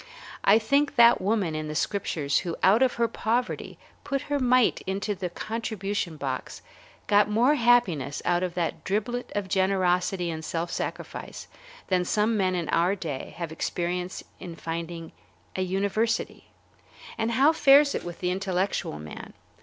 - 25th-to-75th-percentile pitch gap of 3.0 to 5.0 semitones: Yes, average, 4.7 semitones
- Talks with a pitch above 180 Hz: Yes, high, 190 Hz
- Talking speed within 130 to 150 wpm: No, average, 160 wpm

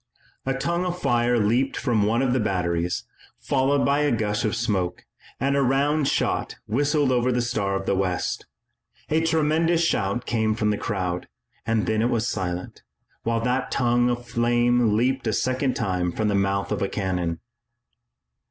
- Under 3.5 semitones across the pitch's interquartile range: No, average, 4.7 semitones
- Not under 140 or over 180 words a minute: Yes, average, 170 wpm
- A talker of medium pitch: No, low, 120 Hz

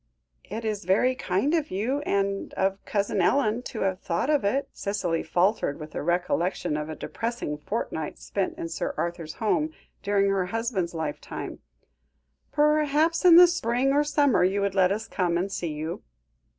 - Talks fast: No, average, 170 wpm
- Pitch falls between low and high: No, high, 200 Hz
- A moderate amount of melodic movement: No, wide, 6.1 semitones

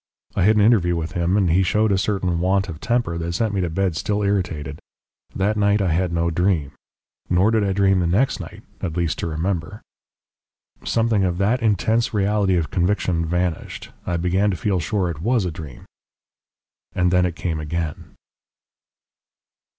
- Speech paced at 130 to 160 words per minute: No, average, 180 wpm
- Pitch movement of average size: Yes, average, 3.3 semitones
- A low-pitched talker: Yes, very low, 90 Hz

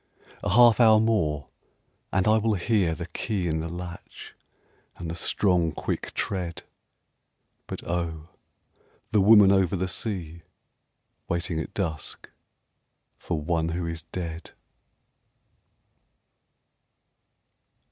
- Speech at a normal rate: No, slow, 110 wpm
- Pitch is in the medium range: No, very low, 90 Hz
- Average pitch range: Yes, average, 3.4 semitones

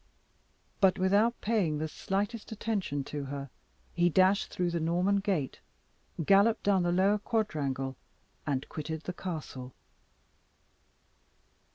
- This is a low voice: No, medium, 180 Hz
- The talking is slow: Yes, slow, 120 wpm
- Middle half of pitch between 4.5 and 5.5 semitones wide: Yes, average, 5.1 semitones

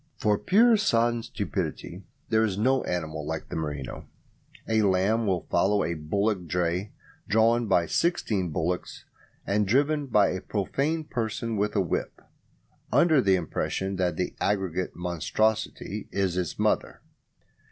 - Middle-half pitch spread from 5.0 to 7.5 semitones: No, average, 4.1 semitones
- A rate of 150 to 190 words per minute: No, average, 140 wpm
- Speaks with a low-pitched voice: Yes, low, 100 Hz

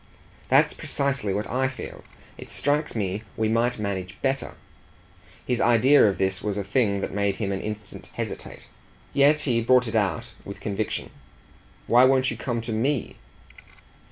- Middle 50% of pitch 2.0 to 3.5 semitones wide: No, average, 4.4 semitones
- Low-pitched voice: Yes, low, 115 Hz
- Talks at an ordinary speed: Yes, average, 160 wpm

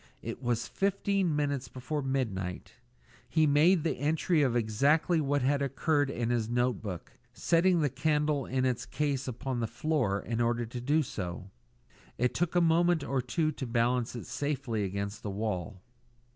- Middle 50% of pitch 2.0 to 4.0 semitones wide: No, average, 4.5 semitones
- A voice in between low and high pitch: No, low, 130 Hz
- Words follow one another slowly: No, average, 165 wpm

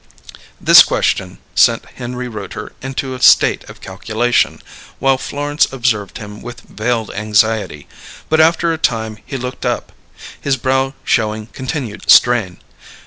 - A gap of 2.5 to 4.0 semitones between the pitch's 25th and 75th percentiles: Yes, average, 3.6 semitones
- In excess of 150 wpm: No, slow, 135 wpm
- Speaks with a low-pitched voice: Yes, low, 120 Hz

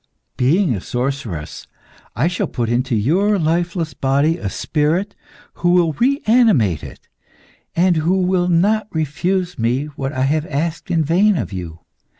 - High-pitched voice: No, medium, 160 Hz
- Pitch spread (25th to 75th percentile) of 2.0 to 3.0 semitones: No, average, 5.2 semitones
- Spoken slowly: No, average, 150 wpm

